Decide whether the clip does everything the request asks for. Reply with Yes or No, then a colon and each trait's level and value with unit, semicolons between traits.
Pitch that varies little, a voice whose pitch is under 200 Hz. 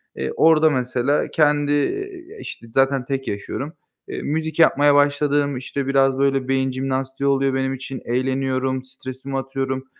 Yes: narrow, 1.6 semitones; low, 135 Hz